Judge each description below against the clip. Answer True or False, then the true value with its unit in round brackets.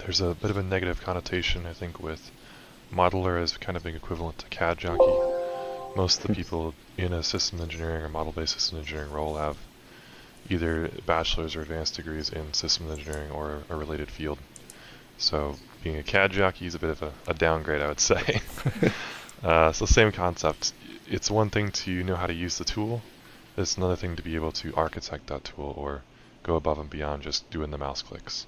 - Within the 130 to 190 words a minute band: False (200 wpm)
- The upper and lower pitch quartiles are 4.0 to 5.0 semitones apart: False (3.2 semitones)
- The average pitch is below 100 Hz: True (85 Hz)